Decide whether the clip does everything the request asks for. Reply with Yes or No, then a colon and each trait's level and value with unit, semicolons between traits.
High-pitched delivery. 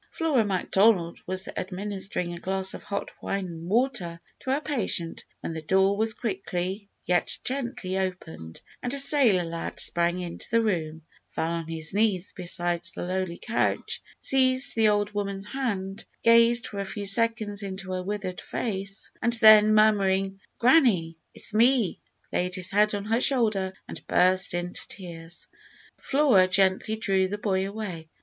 Yes: high, 195 Hz